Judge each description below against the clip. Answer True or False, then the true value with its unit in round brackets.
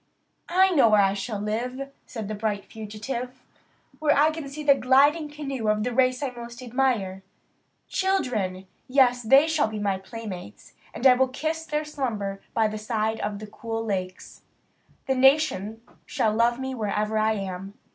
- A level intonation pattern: False (4.3 semitones)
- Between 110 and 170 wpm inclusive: True (165 wpm)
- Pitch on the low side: False (235 Hz)